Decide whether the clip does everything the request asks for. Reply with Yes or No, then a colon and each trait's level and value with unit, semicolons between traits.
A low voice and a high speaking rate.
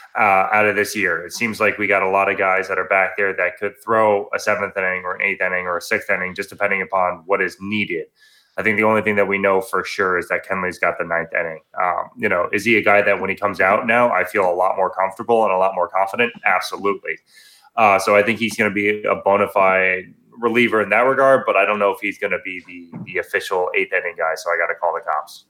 Yes: low, 100 Hz; fast, 275 wpm